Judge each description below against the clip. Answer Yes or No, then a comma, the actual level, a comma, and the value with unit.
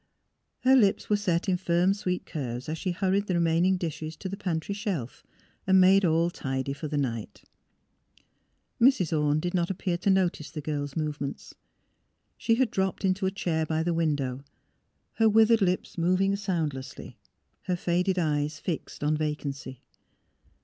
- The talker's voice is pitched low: No, medium, 175 Hz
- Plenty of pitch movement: No, average, 4.0 semitones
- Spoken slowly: No, average, 160 wpm